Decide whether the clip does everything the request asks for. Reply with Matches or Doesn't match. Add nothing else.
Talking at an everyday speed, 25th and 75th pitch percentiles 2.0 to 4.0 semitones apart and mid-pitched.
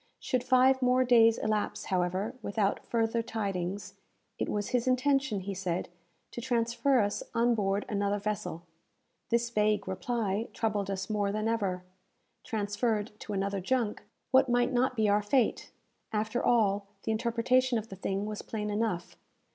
Doesn't match